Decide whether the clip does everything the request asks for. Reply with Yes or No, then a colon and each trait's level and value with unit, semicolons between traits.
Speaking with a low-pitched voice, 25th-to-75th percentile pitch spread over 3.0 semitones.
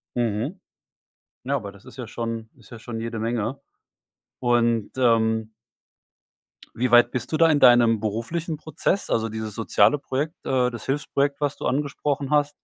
Yes: low, 120 Hz; average, 4.0 semitones